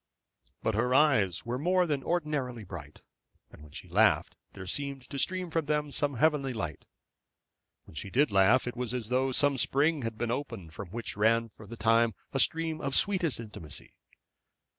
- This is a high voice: No, low, 125 Hz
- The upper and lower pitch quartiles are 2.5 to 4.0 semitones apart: No, average, 5.1 semitones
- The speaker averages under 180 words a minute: No, average, 185 wpm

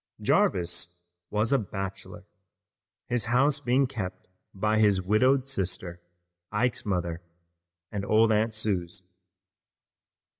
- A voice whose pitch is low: Yes, low, 105 Hz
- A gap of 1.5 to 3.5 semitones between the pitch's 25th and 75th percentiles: No, average, 4.3 semitones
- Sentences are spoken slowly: Yes, slow, 105 wpm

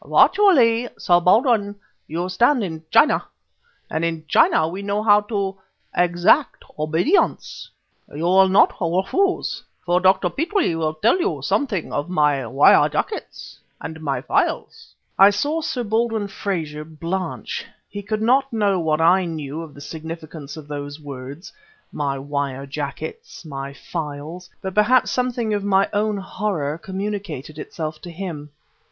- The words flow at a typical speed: Yes, average, 145 wpm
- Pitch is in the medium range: Yes, medium, 180 Hz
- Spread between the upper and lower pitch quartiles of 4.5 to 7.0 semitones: Yes, average, 5.3 semitones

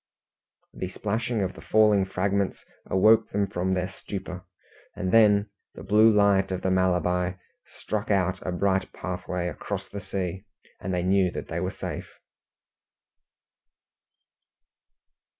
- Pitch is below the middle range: Yes, very low, 95 Hz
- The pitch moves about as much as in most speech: No, narrow, 1.8 semitones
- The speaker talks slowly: Yes, slow, 130 wpm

